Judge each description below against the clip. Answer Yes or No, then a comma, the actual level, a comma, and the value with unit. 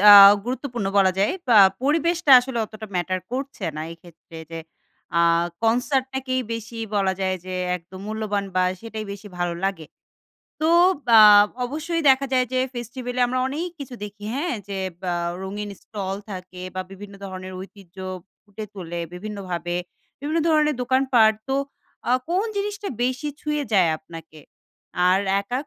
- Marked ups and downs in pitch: Yes, wide, 5.8 semitones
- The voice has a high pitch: Yes, high, 215 Hz